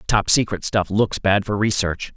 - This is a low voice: Yes, low, 100 Hz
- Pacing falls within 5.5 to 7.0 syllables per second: No, 5.1 syllables/s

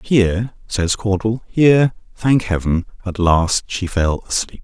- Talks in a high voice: No, low, 100 Hz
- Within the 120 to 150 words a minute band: Yes, average, 140 wpm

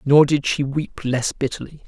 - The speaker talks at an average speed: Yes, average, 190 wpm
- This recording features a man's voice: Yes, male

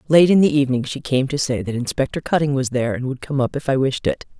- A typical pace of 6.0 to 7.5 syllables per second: Yes, 6.6 syllables/s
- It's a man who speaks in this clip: No, female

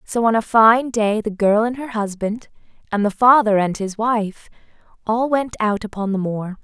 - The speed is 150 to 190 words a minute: No, average, 200 wpm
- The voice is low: No, high, 220 Hz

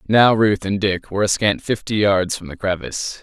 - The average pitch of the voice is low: Yes, low, 100 Hz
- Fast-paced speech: Yes, fast, 225 wpm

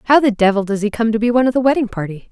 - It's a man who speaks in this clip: No, female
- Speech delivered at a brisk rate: Yes, fast, 340 wpm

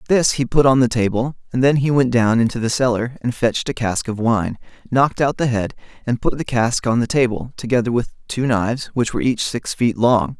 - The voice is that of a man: Yes, male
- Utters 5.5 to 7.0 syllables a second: Yes, 5.6 syllables/s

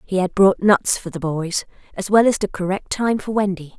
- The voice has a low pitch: No, high, 195 Hz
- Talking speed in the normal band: No, fast, 240 wpm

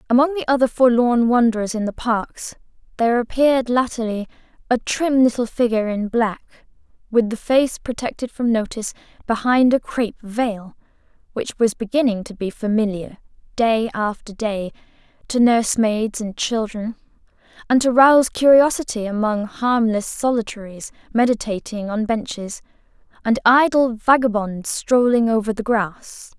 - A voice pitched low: No, high, 230 Hz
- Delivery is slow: Yes, slow, 130 wpm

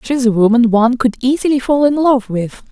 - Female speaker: Yes, female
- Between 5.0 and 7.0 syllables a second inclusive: Yes, 5.6 syllables/s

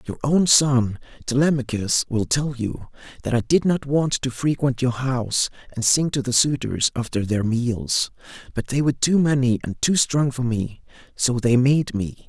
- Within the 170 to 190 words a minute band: Yes, average, 185 wpm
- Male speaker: Yes, male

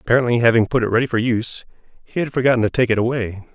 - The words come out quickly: Yes, fast, 235 wpm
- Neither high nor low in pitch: No, low, 120 Hz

